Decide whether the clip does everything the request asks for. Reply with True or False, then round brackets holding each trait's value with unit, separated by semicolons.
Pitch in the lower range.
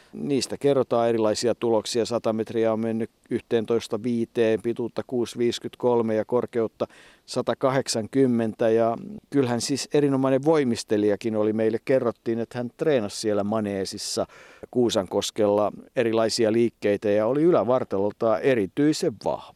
True (115 Hz)